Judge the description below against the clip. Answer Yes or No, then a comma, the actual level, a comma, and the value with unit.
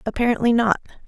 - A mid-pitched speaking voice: No, high, 230 Hz